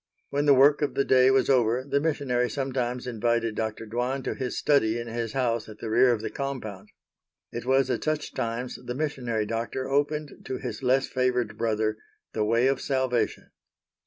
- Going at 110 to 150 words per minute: No, average, 190 wpm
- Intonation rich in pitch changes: No, average, 2.8 semitones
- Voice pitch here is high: No, low, 125 Hz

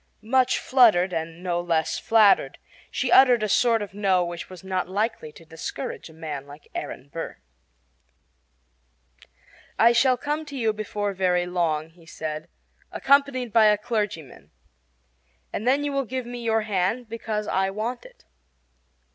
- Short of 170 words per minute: Yes, average, 155 wpm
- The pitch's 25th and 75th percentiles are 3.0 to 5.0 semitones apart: No, wide, 5.6 semitones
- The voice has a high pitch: Yes, high, 205 Hz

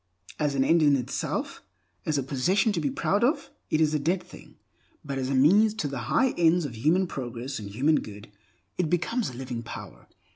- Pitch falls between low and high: Yes, medium, 145 Hz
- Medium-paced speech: No, fast, 210 wpm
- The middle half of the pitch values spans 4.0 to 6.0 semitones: Yes, average, 5.2 semitones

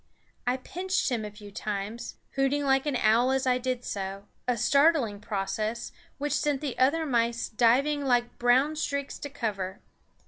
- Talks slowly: No, average, 165 wpm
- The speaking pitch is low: No, very high, 250 Hz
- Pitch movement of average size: Yes, average, 4.4 semitones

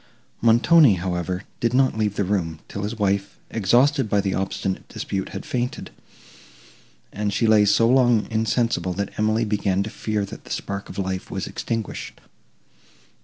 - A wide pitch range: No, average, 2.9 semitones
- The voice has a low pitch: Yes, low, 105 Hz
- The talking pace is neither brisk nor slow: Yes, average, 160 wpm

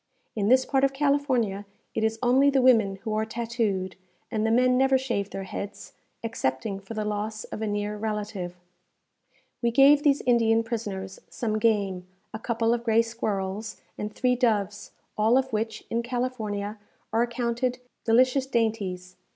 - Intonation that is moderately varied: Yes, average, 3.0 semitones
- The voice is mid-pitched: No, high, 225 Hz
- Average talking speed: Yes, average, 160 wpm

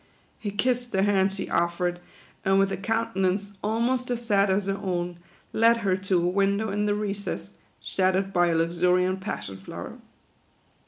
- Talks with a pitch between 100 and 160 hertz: No, high, 195 Hz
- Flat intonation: Yes, narrow, 2.2 semitones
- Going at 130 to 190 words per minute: Yes, average, 165 wpm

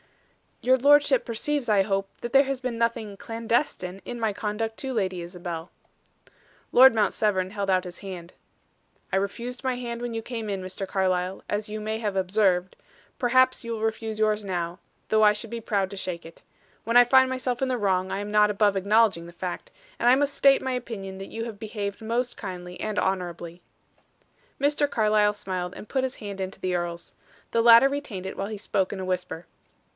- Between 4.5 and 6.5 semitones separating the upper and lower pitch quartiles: No, average, 3.9 semitones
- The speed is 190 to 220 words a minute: Yes, average, 200 wpm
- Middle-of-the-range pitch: No, high, 210 Hz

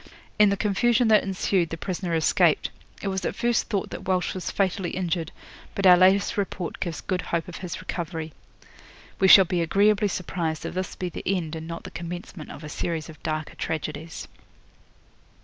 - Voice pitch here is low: No, medium, 180 Hz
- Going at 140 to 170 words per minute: No, average, 185 wpm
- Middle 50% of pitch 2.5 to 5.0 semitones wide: Yes, average, 2.8 semitones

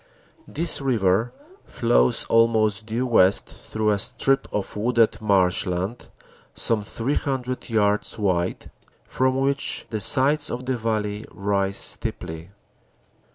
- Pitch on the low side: Yes, low, 110 Hz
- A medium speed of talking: No, slow, 115 wpm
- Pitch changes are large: No, average, 3.7 semitones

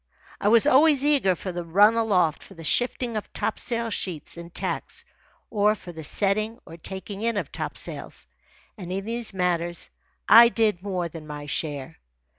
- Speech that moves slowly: No, average, 170 wpm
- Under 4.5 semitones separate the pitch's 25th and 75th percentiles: No, average, 4.8 semitones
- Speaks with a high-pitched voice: Yes, high, 195 Hz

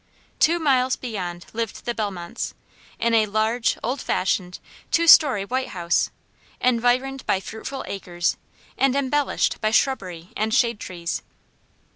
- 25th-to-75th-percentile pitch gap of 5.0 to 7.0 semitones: Yes, average, 5.3 semitones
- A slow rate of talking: Yes, slow, 130 wpm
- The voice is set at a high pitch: Yes, high, 225 Hz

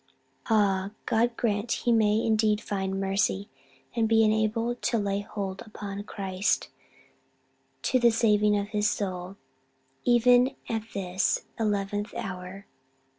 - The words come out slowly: Yes, slow, 125 wpm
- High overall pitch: Yes, high, 210 Hz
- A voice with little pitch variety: Yes, narrow, 2.3 semitones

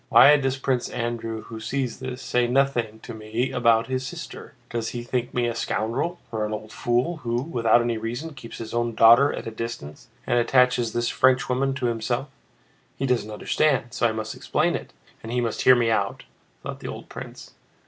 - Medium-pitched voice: No, low, 120 Hz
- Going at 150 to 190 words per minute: No, average, 200 wpm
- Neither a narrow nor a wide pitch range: No, narrow, 2.3 semitones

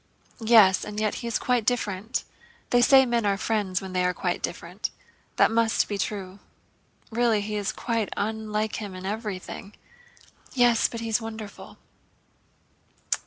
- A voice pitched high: Yes, high, 215 Hz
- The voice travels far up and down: No, narrow, 2.4 semitones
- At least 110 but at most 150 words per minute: Yes, average, 145 wpm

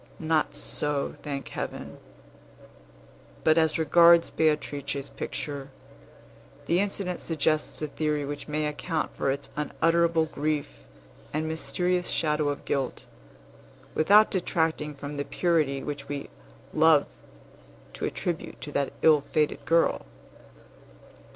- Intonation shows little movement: Yes, narrow, 2.2 semitones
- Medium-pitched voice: Yes, medium, 155 Hz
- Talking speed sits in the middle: No, slow, 115 wpm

